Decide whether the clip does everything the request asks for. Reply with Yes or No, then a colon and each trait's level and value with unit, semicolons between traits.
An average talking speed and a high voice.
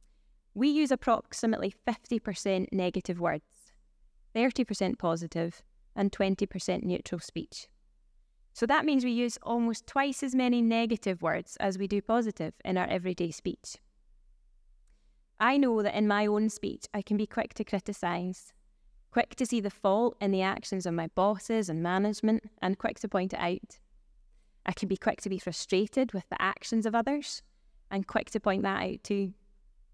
Yes: average, 165 wpm; high, 205 Hz